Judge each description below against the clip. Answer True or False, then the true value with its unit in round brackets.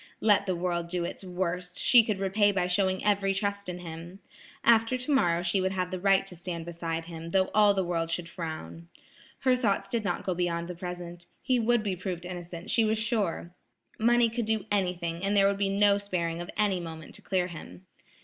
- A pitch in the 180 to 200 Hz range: True (185 Hz)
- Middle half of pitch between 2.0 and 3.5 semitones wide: True (2.9 semitones)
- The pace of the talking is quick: True (210 wpm)